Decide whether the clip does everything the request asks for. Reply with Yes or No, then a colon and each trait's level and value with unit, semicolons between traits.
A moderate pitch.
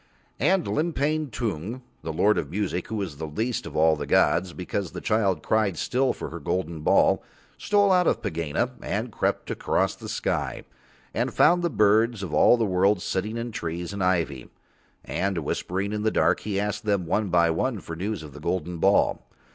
No: low, 100 Hz